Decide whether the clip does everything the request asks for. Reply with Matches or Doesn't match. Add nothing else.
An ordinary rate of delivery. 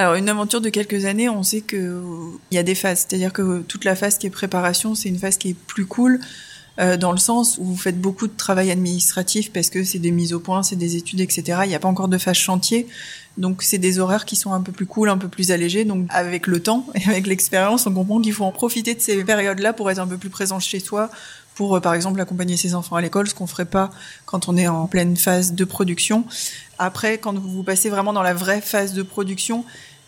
Doesn't match